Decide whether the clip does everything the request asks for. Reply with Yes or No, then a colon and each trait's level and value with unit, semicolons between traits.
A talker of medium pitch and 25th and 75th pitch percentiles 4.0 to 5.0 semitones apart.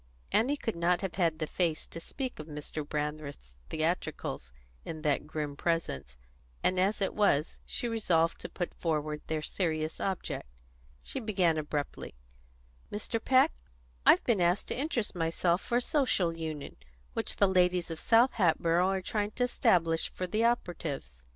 Yes: medium, 170 Hz; average, 4.7 semitones